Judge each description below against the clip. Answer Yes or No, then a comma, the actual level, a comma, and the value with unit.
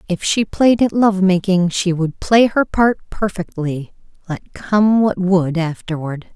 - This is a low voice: No, high, 190 Hz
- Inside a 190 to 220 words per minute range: No, average, 160 wpm